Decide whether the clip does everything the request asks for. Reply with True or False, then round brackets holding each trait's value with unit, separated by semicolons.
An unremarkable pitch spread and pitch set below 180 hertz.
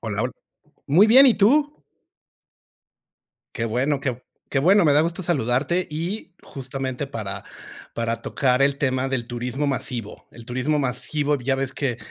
True (3.6 semitones; 135 Hz)